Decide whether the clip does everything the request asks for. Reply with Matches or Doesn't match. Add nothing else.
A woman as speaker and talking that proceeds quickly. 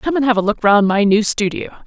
Matches